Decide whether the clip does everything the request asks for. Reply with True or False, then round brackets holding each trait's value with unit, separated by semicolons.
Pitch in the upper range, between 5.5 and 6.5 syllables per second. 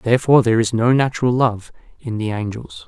False (115 Hz; 6.3 syllables/s)